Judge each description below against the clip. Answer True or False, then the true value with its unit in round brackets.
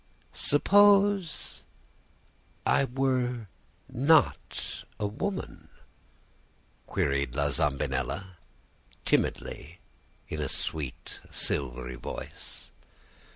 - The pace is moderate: False (65 wpm)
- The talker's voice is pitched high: False (95 Hz)